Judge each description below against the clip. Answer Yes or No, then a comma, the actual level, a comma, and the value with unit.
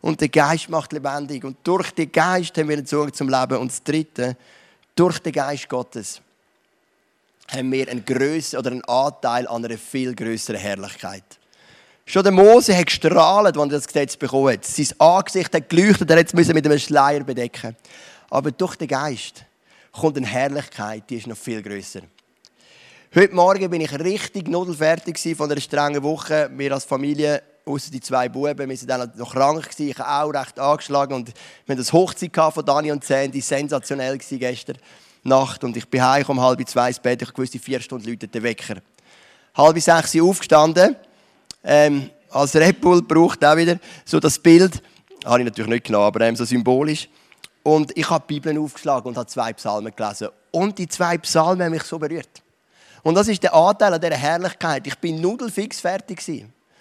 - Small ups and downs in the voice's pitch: No, average, 4.4 semitones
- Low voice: No, medium, 145 Hz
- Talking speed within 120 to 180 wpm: No, average, 190 wpm